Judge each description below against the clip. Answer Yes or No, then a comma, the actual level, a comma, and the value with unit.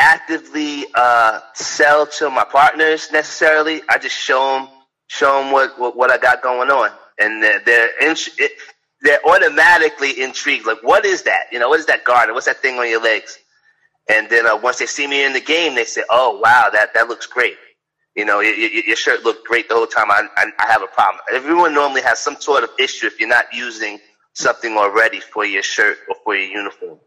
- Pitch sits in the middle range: Yes, medium, 175 Hz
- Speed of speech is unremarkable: No, fast, 215 wpm